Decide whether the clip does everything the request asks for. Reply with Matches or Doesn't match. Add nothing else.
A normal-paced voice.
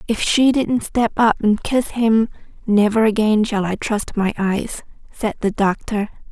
Matches